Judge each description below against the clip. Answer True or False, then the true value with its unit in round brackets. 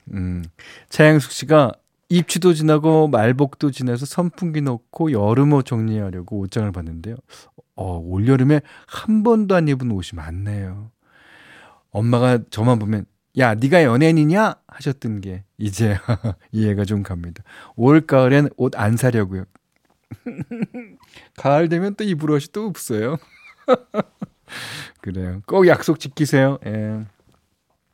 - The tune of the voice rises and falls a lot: True (6.9 semitones)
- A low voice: True (125 Hz)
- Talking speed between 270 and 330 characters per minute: False (250 characters per minute)